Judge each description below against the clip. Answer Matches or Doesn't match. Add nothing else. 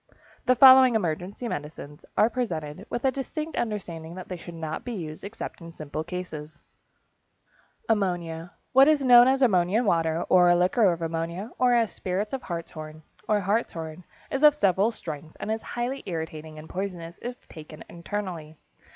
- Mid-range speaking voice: Matches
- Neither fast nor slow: Matches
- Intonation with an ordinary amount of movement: Doesn't match